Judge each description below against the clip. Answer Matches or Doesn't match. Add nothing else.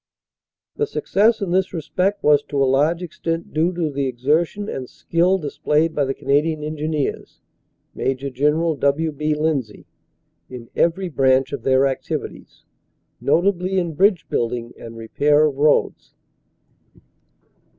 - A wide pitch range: Doesn't match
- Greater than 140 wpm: Doesn't match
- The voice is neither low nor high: Matches